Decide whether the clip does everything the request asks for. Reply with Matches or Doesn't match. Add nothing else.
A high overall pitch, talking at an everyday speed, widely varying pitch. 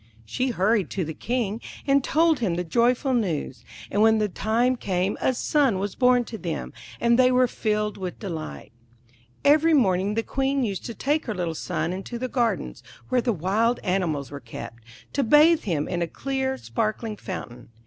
Matches